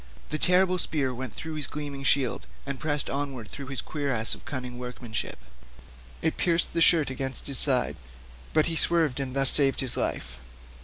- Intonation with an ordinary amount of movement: Yes, average, 3.1 semitones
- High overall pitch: No, medium, 140 Hz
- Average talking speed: Yes, average, 175 wpm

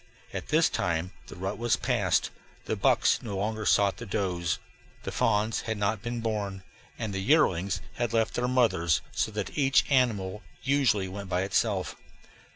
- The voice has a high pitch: No, low, 105 Hz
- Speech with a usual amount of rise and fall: Yes, average, 3.4 semitones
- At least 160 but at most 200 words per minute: Yes, average, 165 wpm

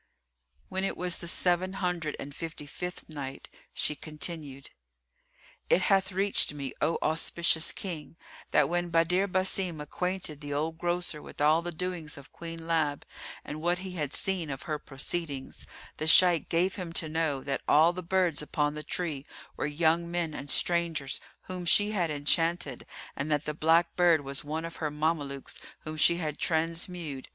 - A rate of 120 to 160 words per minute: No, average, 170 wpm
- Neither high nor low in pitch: Yes, medium, 165 Hz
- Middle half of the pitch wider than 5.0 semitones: No, average, 2.9 semitones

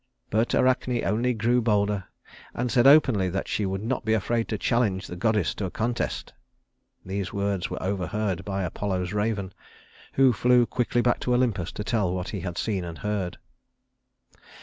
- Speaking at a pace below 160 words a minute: No, average, 170 wpm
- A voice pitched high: No, low, 105 Hz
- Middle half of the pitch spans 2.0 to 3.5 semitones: No, average, 3.9 semitones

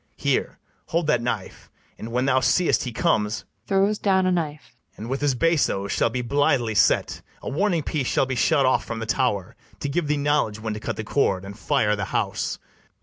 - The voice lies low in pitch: Yes, low, 130 Hz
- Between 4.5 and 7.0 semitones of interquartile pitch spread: Yes, average, 5.3 semitones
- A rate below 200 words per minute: No, fast, 205 wpm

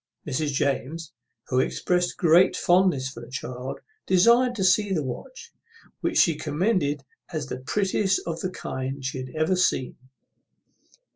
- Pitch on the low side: No, medium, 160 Hz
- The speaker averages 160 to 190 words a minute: No, average, 145 wpm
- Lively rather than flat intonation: Yes, wide, 5.8 semitones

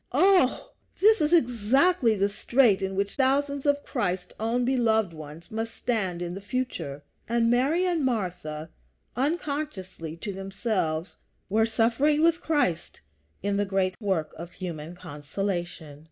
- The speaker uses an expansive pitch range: Yes, wide, 6.8 semitones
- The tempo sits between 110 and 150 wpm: Yes, average, 140 wpm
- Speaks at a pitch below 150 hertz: No, high, 215 Hz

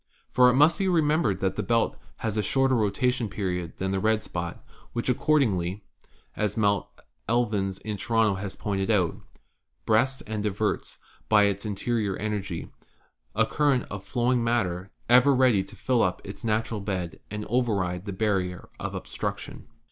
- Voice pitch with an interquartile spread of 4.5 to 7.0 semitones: No, average, 3.7 semitones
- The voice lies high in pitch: No, low, 105 Hz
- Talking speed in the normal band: Yes, average, 165 wpm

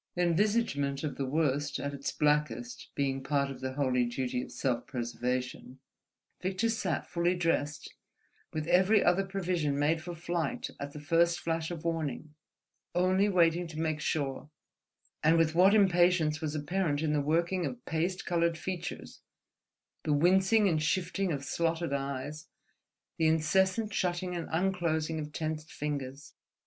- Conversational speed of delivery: Yes, average, 150 wpm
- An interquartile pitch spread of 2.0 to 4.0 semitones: Yes, average, 3.6 semitones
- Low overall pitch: No, medium, 160 Hz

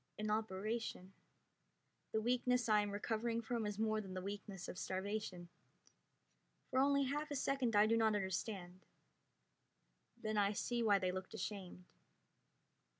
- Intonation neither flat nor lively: Yes, average, 3.1 semitones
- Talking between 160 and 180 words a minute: No, average, 145 wpm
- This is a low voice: No, high, 215 Hz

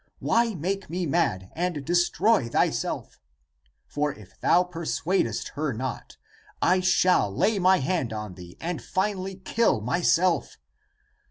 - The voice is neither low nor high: Yes, medium, 175 Hz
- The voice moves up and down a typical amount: No, wide, 6.6 semitones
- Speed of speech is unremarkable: No, slow, 125 wpm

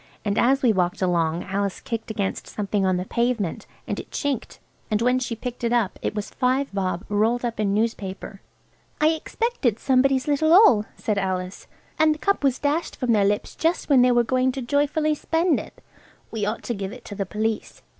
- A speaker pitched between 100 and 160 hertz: No, high, 230 Hz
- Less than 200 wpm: No, fast, 205 wpm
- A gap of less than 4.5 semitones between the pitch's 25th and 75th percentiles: No, average, 5.1 semitones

